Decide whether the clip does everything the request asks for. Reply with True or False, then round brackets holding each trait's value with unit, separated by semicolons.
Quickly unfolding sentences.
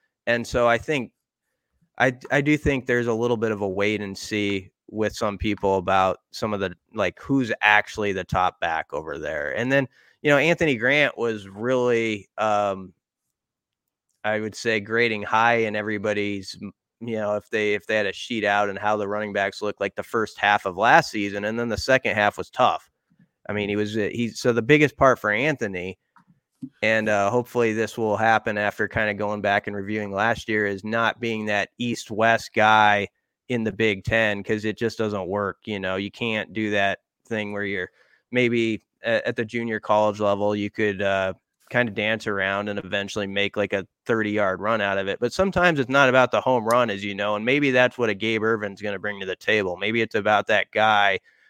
True (210 wpm)